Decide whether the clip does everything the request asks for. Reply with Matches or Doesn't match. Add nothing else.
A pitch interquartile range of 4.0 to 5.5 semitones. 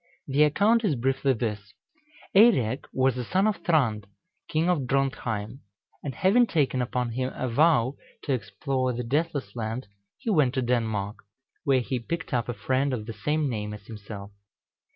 Matches